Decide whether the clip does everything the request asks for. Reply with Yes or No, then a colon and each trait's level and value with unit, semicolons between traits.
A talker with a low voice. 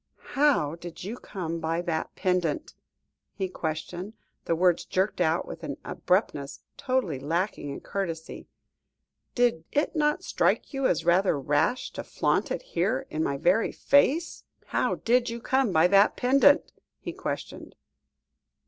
No: medium, 185 Hz